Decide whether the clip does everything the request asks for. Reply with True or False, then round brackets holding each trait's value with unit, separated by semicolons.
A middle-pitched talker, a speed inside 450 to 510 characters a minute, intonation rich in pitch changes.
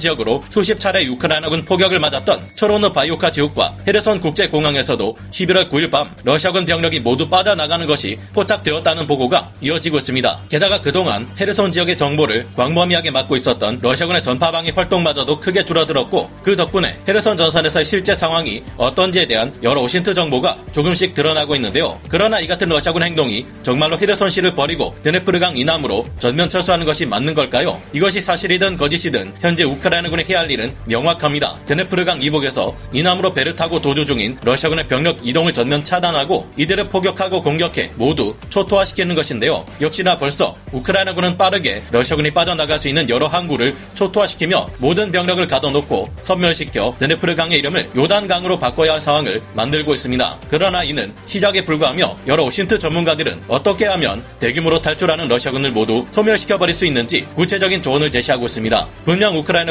False (165 Hz; 455 characters per minute; 4.4 semitones)